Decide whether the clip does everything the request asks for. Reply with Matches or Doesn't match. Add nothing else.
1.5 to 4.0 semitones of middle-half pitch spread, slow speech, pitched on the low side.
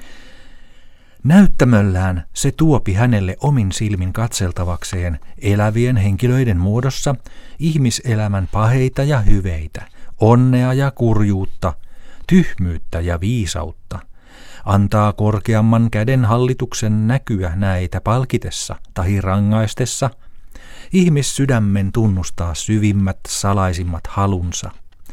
Doesn't match